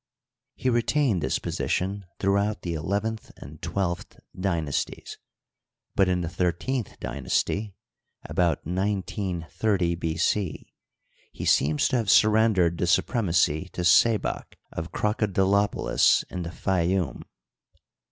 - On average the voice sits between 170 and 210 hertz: No, very low, 95 Hz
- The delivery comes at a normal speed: No, slow, 115 wpm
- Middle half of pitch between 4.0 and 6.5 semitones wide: No, average, 3.5 semitones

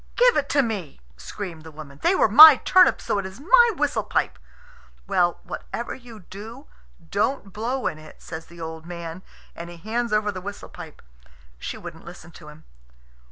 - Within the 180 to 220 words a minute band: Yes, average, 190 wpm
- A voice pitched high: Yes, high, 200 Hz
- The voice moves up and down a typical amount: No, wide, 6.6 semitones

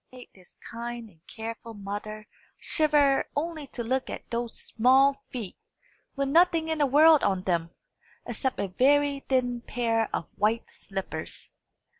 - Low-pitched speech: No, high, 240 Hz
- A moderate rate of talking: Yes, average, 150 wpm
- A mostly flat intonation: No, average, 4.7 semitones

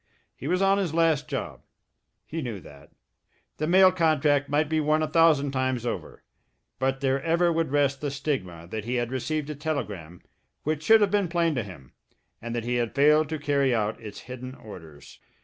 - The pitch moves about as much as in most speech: Yes, average, 4.7 semitones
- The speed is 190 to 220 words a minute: Yes, average, 195 wpm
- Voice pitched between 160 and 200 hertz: No, medium, 140 Hz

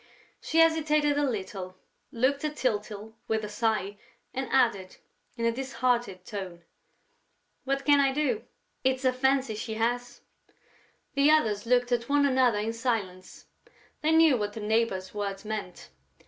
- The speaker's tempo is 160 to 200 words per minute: No, average, 145 wpm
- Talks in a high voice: Yes, high, 235 Hz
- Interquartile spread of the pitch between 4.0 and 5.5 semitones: Yes, average, 4.5 semitones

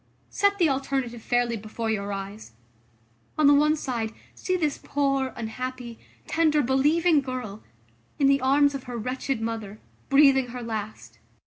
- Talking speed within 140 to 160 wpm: Yes, average, 145 wpm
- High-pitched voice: Yes, very high, 260 Hz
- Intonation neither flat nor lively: Yes, average, 3.9 semitones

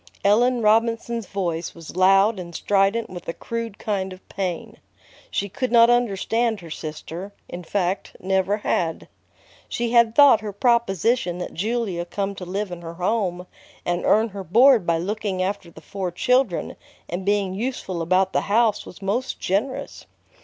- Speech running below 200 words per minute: Yes, average, 160 wpm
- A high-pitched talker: Yes, high, 200 Hz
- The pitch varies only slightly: No, average, 4.0 semitones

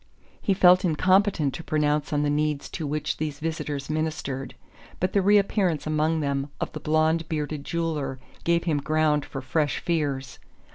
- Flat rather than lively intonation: Yes, narrow, 2.2 semitones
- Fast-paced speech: No, average, 160 wpm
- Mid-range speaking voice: Yes, medium, 155 Hz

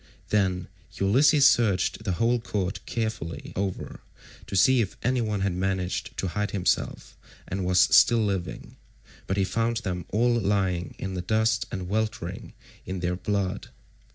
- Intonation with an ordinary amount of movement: Yes, average, 3.4 semitones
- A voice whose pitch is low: Yes, low, 100 Hz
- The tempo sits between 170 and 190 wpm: No, average, 150 wpm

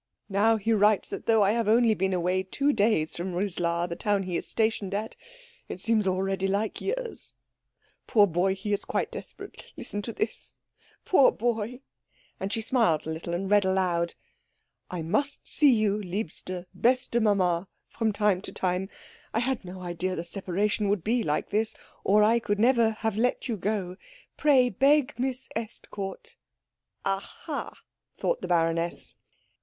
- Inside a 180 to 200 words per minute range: No, average, 170 wpm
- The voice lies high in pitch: Yes, high, 205 Hz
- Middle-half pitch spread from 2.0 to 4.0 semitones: Yes, average, 3.5 semitones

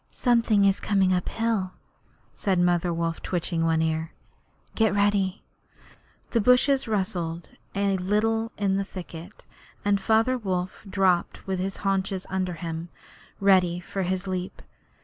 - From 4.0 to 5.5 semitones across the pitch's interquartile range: No, narrow, 2.4 semitones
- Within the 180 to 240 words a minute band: No, slow, 135 wpm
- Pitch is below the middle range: No, high, 190 Hz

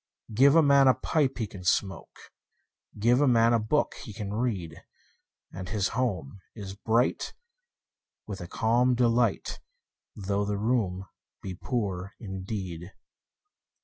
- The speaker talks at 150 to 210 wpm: No, average, 140 wpm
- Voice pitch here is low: Yes, low, 105 Hz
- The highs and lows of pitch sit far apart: No, average, 4.2 semitones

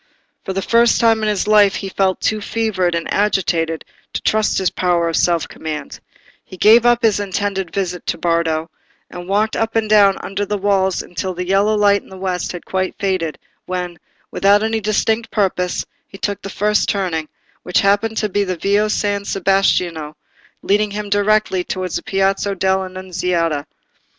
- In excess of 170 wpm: Yes, average, 180 wpm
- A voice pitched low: No, high, 195 Hz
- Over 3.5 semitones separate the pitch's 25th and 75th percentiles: No, narrow, 2.5 semitones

